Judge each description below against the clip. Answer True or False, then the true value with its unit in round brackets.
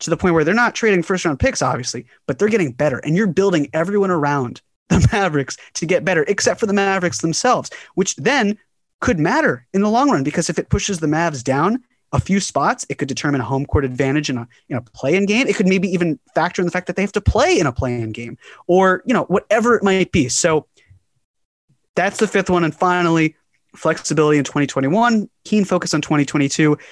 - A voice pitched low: False (165 Hz)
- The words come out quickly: True (220 wpm)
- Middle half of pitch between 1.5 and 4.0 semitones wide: False (5.6 semitones)